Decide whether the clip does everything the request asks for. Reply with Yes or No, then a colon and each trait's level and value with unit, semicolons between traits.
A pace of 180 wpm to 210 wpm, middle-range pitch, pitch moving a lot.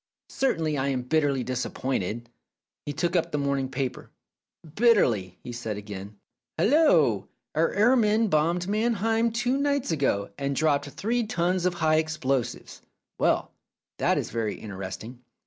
No: average, 145 wpm; medium, 155 Hz; wide, 8.7 semitones